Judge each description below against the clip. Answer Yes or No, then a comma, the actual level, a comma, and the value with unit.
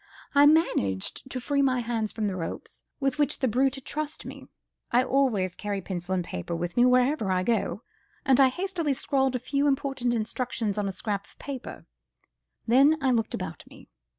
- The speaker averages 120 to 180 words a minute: No, average, 190 wpm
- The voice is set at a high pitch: Yes, very high, 250 Hz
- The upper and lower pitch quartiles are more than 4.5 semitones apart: Yes, average, 5.0 semitones